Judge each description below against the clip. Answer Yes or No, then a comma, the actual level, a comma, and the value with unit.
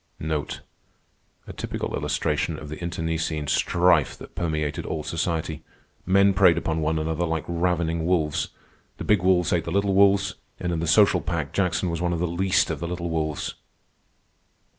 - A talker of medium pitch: No, very low, 85 Hz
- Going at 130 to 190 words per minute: Yes, average, 165 wpm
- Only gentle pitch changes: Yes, narrow, 2.0 semitones